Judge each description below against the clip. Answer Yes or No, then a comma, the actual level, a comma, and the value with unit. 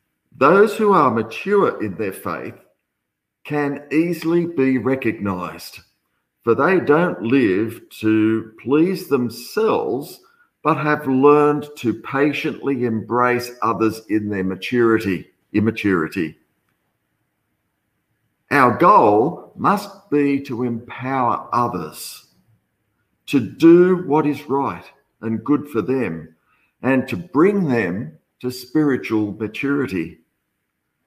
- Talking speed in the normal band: No, slow, 100 wpm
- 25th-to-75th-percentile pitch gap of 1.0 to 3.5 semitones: No, average, 5.0 semitones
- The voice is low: Yes, low, 130 Hz